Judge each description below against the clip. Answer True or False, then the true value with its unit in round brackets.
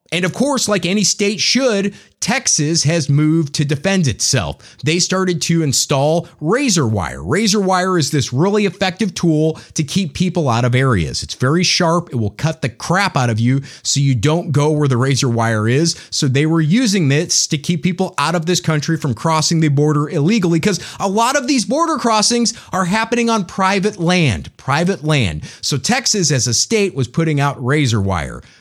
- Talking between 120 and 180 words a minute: False (195 wpm)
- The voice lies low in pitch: False (165 Hz)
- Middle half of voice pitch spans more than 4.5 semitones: True (5.3 semitones)